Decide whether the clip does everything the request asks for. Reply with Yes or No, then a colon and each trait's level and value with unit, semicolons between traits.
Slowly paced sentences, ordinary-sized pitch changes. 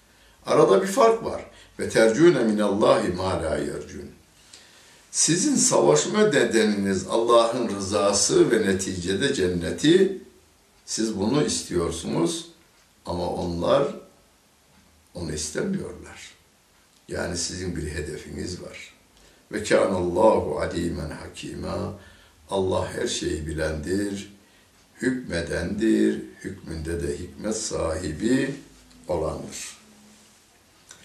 Yes: slow, 80 wpm; average, 4.2 semitones